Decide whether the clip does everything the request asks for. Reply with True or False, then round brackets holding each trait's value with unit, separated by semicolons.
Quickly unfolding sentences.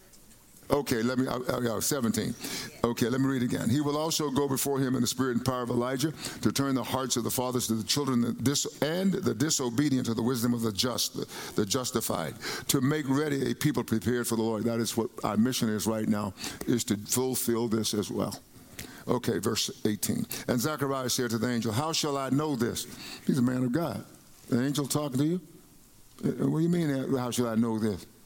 True (225 wpm)